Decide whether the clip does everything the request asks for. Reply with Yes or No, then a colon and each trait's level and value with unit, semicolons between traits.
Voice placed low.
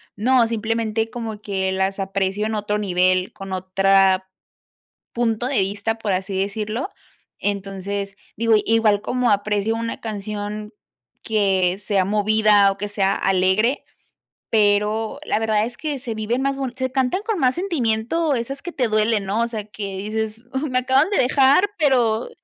No: high, 215 Hz